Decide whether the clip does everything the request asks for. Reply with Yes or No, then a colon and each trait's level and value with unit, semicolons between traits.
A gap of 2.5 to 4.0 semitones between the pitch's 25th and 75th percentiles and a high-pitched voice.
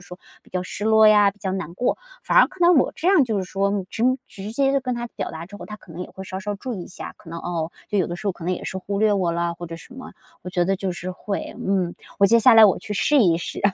Yes: average, 3.5 semitones; high, 195 Hz